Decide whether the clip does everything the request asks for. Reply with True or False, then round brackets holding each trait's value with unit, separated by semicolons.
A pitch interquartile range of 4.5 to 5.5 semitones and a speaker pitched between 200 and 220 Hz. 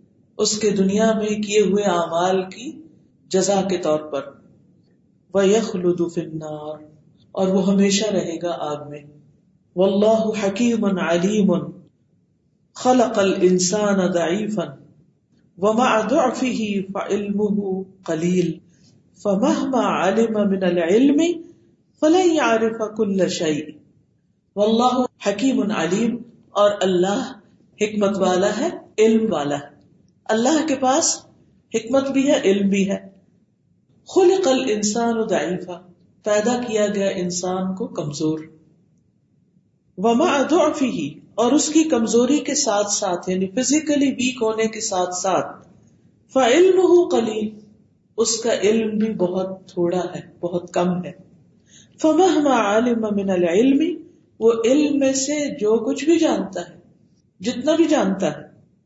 True (4.9 semitones; 205 Hz)